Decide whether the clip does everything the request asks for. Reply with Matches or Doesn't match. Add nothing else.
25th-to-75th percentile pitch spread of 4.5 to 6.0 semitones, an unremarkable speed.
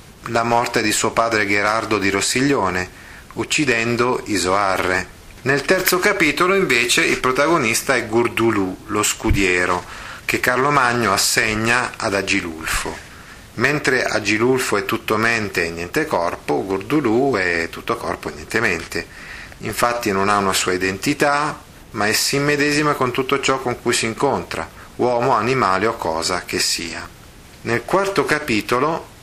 Matches